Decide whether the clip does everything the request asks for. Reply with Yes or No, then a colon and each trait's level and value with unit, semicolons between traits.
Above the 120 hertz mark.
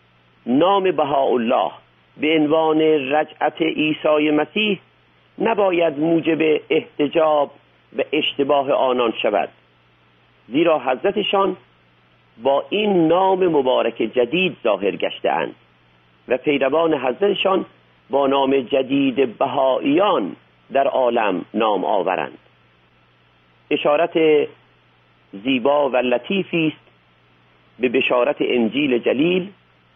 Yes: low, 135 Hz